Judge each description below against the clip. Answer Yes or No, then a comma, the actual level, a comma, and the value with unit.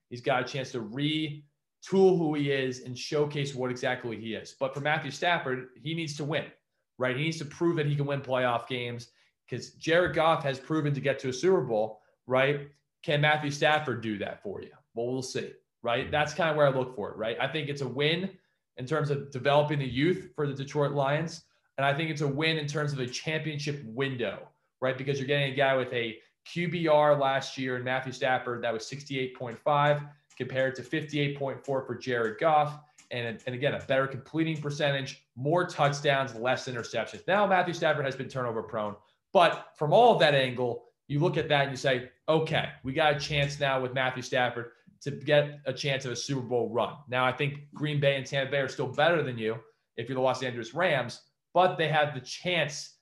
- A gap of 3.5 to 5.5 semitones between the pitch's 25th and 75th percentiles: No, average, 2.8 semitones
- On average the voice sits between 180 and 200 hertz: No, medium, 140 Hz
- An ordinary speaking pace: No, fast, 215 wpm